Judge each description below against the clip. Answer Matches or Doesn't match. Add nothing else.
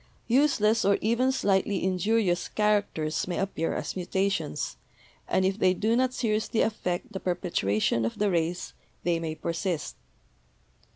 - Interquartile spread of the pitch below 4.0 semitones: Matches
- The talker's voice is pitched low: Doesn't match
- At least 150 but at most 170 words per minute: Doesn't match